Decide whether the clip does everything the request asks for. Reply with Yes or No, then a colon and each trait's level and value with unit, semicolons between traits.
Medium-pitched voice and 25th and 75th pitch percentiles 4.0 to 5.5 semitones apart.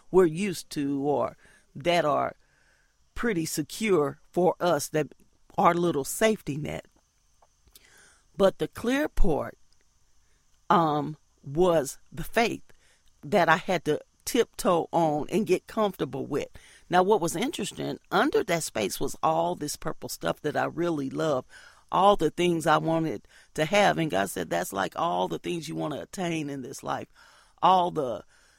Yes: medium, 160 Hz; average, 4.3 semitones